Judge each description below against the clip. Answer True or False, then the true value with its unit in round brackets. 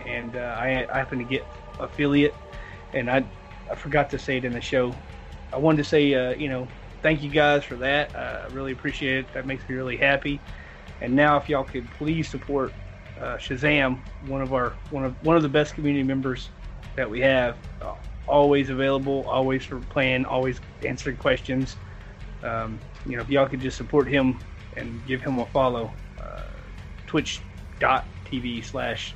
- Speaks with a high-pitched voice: False (130 Hz)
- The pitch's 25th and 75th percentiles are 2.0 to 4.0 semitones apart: True (2.8 semitones)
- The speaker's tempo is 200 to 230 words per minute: False (180 wpm)